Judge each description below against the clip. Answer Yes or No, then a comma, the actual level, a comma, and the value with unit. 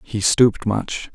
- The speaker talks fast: No, average, 155 wpm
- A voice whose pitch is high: No, low, 110 Hz